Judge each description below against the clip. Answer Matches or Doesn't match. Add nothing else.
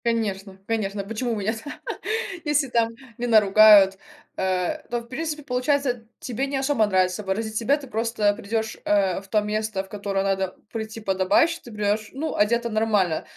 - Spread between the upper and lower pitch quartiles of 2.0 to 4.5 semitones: Matches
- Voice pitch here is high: Matches